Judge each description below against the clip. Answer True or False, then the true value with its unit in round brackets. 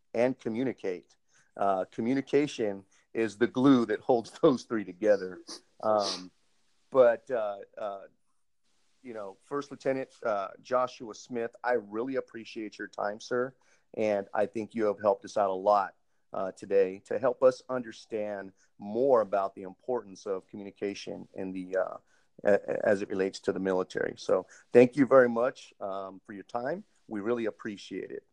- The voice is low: True (110 Hz)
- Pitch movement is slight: False (4.5 semitones)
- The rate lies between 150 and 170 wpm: True (155 wpm)